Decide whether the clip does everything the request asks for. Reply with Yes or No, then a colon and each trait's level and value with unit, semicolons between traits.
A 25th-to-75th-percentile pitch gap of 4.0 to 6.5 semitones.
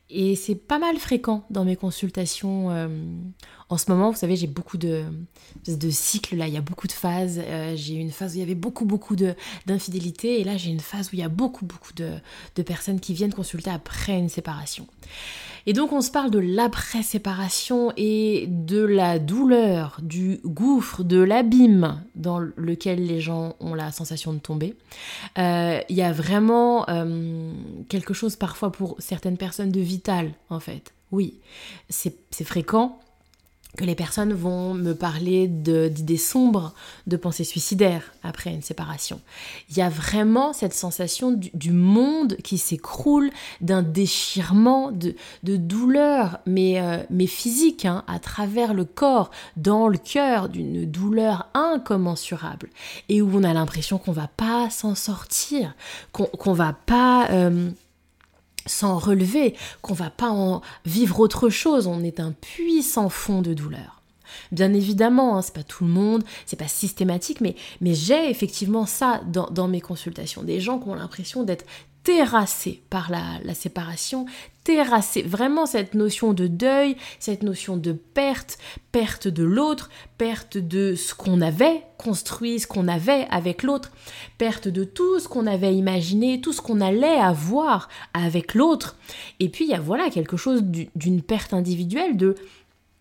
Yes: average, 4.4 semitones